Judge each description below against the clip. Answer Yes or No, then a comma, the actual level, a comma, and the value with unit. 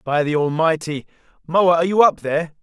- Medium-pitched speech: Yes, medium, 160 Hz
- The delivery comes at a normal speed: Yes, average, 185 wpm